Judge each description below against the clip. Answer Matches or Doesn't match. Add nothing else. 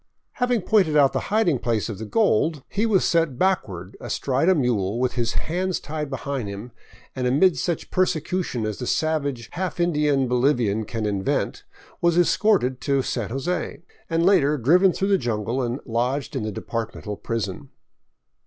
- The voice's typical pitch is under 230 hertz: Matches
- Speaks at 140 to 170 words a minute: Matches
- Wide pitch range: Matches